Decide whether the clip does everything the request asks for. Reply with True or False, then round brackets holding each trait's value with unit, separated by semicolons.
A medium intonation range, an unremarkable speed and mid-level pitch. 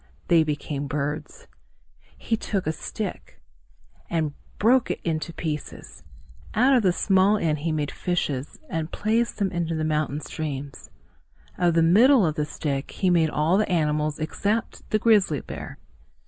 True (4.9 semitones; 155 wpm; 165 Hz)